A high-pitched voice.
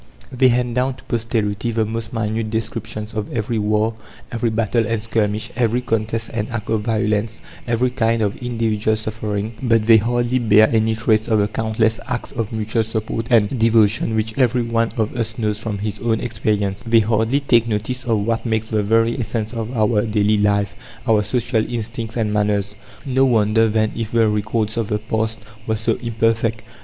No: low, 110 Hz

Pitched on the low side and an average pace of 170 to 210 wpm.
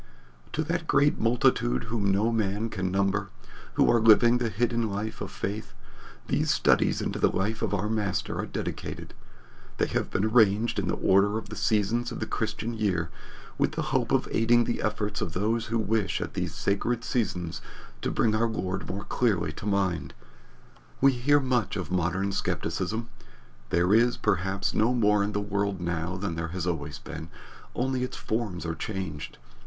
Yes: low, 105 Hz; average, 180 wpm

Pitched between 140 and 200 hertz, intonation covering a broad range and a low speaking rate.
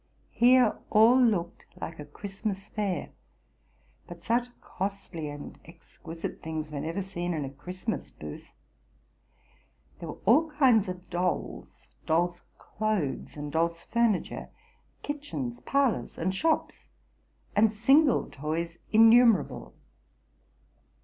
Yes: high, 190 Hz; wide, 5.7 semitones; slow, 110 wpm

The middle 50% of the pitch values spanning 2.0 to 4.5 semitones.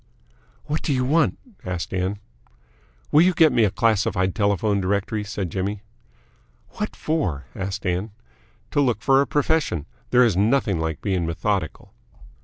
No: wide, 5.5 semitones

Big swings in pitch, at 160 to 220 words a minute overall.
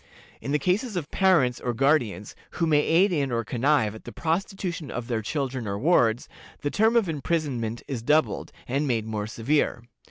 Yes: wide, 5.8 semitones; average, 185 wpm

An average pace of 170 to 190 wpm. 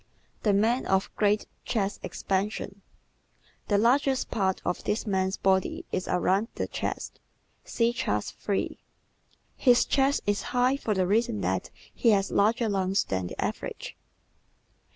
No: average, 145 wpm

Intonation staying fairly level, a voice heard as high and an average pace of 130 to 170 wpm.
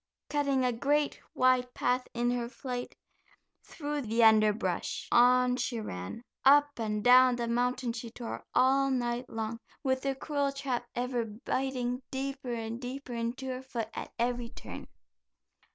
Yes: narrow, 2.1 semitones; very high, 250 Hz; average, 150 wpm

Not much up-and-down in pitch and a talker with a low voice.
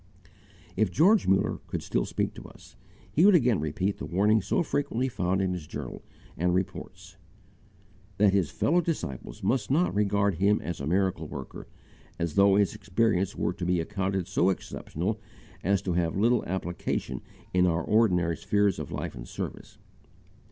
No: average, 3.1 semitones; very low, 95 Hz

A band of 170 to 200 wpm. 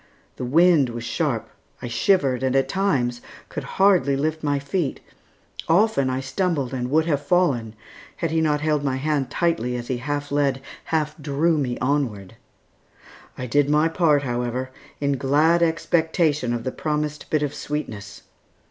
No: average, 160 wpm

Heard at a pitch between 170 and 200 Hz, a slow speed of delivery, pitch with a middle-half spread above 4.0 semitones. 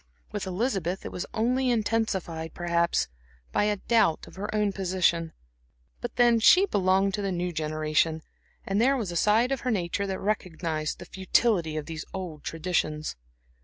No: high, 190 Hz; average, 165 wpm; average, 4.4 semitones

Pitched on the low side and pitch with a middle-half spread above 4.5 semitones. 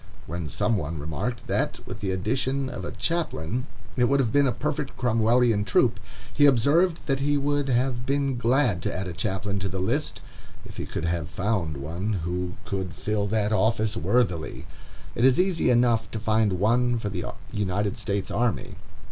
Yes: low, 110 Hz; average, 5.1 semitones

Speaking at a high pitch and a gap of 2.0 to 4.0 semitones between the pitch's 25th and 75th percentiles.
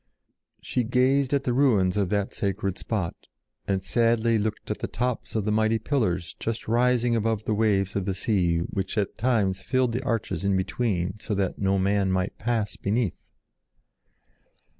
No: low, 105 Hz; average, 3.4 semitones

